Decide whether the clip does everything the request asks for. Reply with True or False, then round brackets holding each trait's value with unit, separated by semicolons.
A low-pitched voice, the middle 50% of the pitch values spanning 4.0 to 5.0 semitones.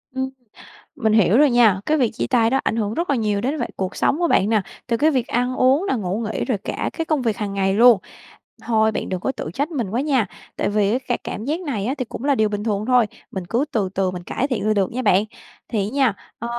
False (230 Hz; 4.3 semitones)